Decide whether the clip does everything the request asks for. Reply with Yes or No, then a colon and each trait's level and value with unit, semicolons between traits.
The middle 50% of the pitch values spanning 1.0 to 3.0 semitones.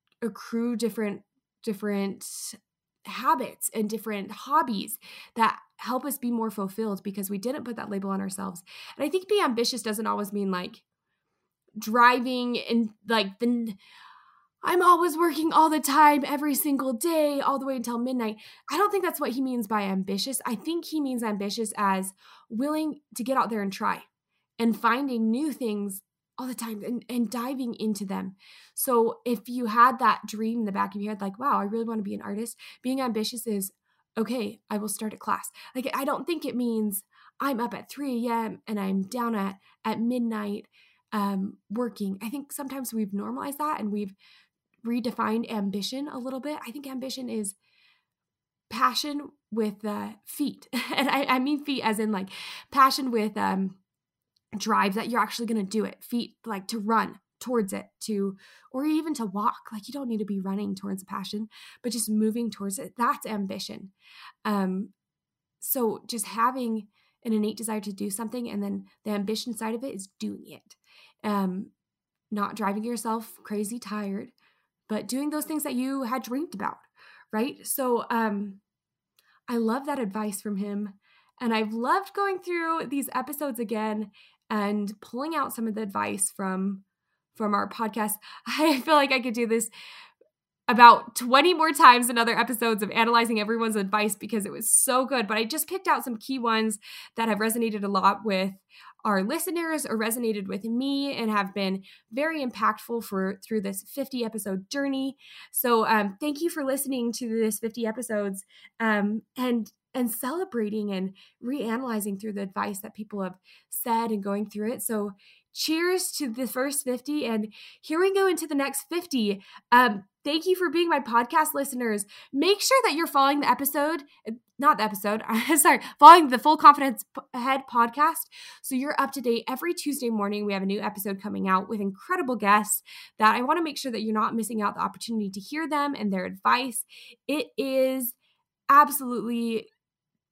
No: average, 4.3 semitones